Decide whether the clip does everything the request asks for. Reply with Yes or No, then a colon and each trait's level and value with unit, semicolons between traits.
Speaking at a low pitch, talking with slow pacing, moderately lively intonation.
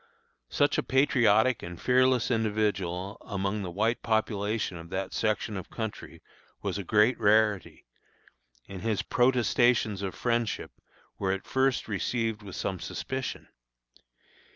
Yes: low, 110 Hz; slow, 130 wpm; average, 3.3 semitones